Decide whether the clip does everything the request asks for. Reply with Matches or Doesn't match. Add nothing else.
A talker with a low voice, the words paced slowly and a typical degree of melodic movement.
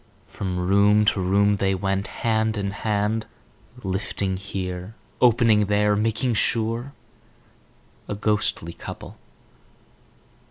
Doesn't match